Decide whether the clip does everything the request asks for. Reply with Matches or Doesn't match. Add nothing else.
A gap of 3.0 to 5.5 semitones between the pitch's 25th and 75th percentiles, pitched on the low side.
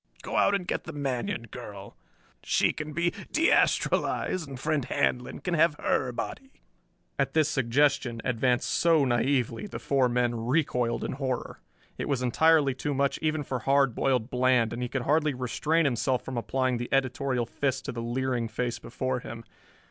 Matches